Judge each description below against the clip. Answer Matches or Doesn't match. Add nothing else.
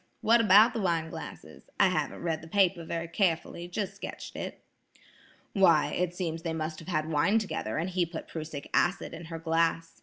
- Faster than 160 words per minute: Matches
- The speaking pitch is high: Doesn't match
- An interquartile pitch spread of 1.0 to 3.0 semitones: Matches